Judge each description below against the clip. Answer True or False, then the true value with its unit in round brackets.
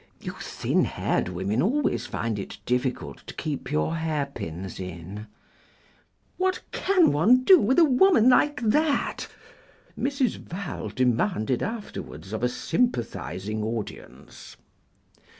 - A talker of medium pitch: True (145 Hz)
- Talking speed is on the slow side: True (115 wpm)